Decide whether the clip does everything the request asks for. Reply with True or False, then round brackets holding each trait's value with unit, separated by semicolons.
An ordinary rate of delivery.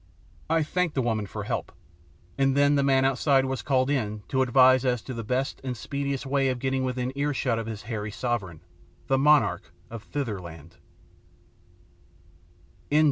True (160 wpm)